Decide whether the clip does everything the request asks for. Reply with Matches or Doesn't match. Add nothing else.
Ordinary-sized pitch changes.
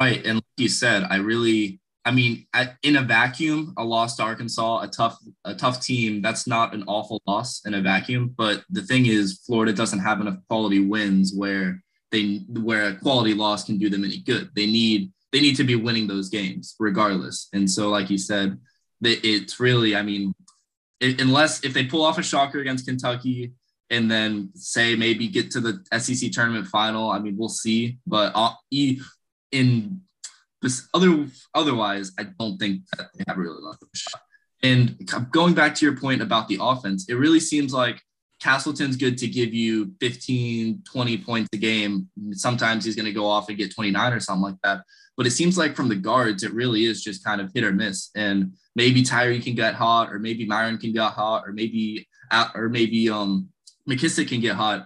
Matches